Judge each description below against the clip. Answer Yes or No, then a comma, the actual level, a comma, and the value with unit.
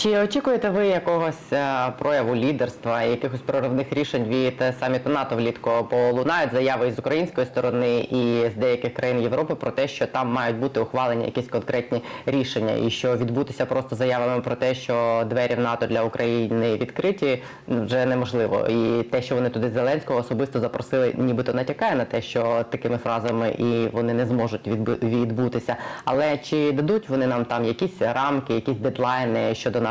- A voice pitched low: Yes, low, 125 Hz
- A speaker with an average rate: No, fast, 165 wpm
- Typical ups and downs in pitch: No, narrow, 2.2 semitones